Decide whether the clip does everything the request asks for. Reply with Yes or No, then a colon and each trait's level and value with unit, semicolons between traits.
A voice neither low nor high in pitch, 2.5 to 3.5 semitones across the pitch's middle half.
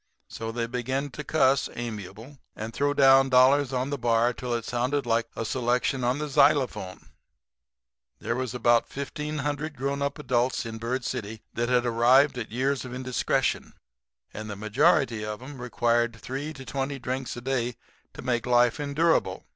No: low, 125 Hz; average, 2.8 semitones